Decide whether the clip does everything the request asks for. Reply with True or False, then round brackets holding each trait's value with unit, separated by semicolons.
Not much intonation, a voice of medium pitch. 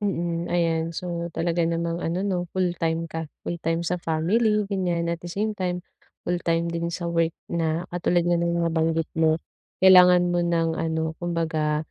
True (1.3 semitones; 170 Hz)